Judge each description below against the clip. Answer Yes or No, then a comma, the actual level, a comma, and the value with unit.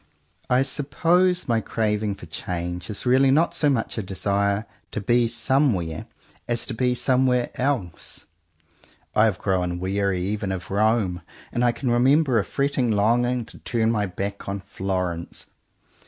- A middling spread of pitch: Yes, average, 4.4 semitones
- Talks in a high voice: No, low, 110 Hz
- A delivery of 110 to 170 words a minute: Yes, average, 155 wpm